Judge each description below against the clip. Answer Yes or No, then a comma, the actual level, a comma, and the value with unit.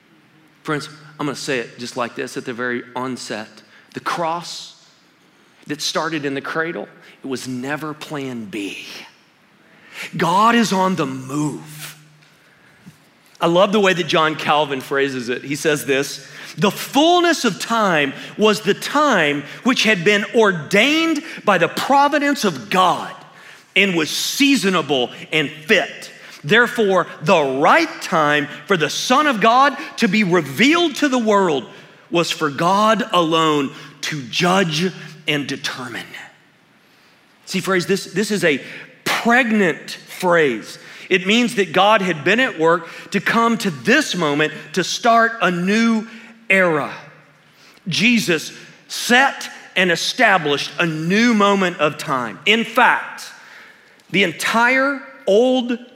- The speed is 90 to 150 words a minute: Yes, slow, 135 wpm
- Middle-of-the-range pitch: Yes, medium, 180 Hz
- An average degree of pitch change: No, wide, 6.8 semitones